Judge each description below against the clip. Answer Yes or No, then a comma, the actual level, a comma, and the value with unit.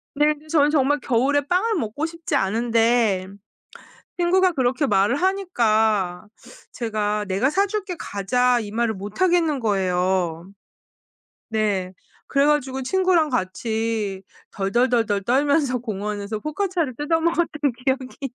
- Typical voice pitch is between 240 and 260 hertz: Yes, high, 245 Hz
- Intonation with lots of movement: Yes, wide, 6.2 semitones